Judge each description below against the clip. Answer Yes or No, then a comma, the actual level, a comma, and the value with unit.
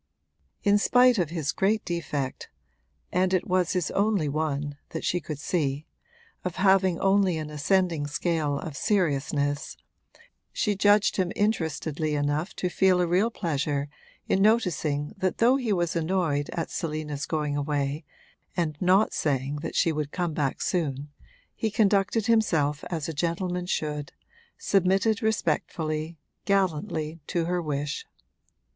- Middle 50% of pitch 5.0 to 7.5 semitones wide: No, average, 4.3 semitones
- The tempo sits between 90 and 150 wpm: Yes, average, 140 wpm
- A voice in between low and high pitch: Yes, medium, 170 Hz